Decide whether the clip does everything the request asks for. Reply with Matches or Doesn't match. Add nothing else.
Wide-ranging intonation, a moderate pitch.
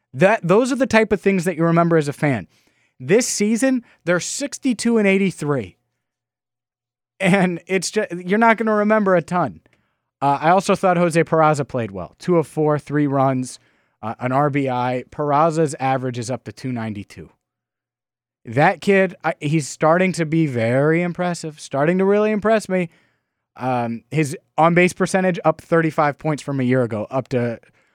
Matches